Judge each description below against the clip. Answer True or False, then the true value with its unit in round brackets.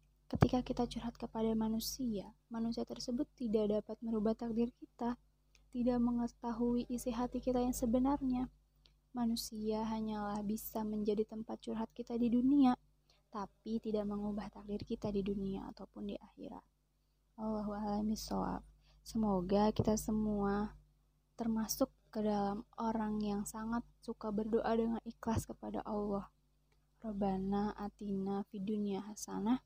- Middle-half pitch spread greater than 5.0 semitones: False (2.4 semitones)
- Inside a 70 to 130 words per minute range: True (115 wpm)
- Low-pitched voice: False (220 Hz)